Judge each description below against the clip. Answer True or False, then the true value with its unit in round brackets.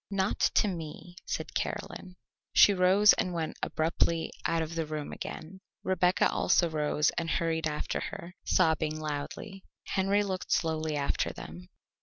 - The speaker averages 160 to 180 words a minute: False (145 wpm)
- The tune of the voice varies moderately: True (3.2 semitones)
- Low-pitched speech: False (165 Hz)